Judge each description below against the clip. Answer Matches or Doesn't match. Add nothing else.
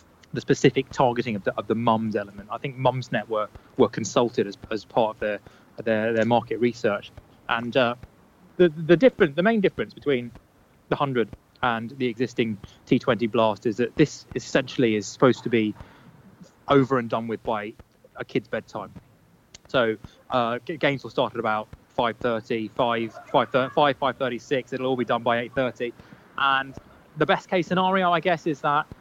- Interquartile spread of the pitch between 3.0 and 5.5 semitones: Matches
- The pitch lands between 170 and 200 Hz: Doesn't match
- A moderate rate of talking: Matches